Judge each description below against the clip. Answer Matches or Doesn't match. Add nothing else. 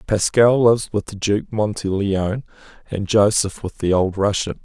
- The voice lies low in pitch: Matches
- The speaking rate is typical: Matches